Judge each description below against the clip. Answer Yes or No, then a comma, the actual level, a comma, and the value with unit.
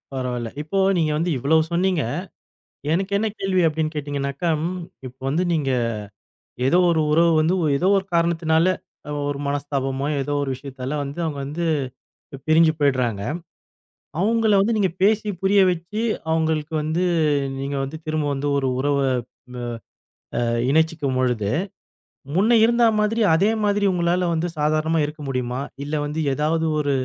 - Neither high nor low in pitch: Yes, medium, 155 Hz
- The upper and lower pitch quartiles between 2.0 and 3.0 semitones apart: No, average, 4.0 semitones